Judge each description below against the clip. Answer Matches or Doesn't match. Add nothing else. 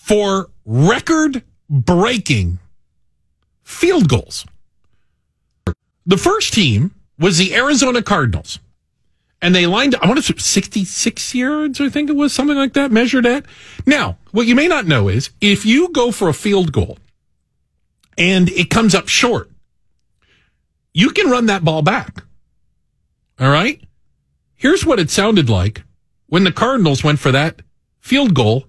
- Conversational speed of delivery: Matches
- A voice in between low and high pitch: Doesn't match